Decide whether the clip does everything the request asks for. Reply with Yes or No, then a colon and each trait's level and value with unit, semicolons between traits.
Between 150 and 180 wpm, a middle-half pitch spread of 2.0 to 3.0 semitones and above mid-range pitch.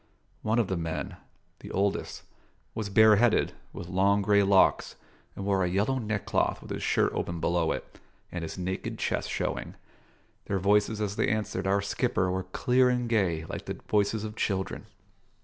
No: average, 170 wpm; narrow, 2.6 semitones; low, 100 Hz